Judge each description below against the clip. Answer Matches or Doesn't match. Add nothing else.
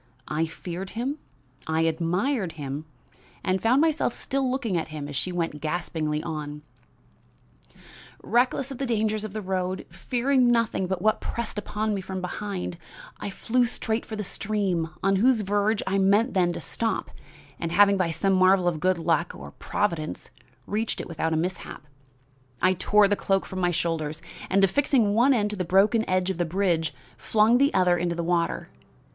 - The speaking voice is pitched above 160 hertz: Matches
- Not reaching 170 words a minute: Doesn't match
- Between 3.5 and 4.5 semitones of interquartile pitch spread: Matches